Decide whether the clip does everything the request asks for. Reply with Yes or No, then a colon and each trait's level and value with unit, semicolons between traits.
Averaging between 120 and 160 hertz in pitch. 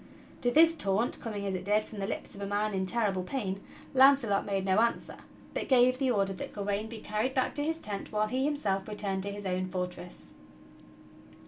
No: high, 210 Hz